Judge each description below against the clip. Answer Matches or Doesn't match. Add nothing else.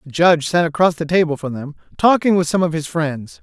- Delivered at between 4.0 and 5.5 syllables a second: Doesn't match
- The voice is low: Doesn't match